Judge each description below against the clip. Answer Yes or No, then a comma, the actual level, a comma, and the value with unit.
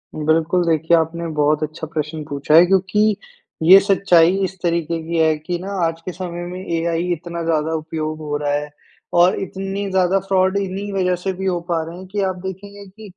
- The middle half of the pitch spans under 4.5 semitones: Yes, average, 2.9 semitones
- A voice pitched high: No, medium, 175 Hz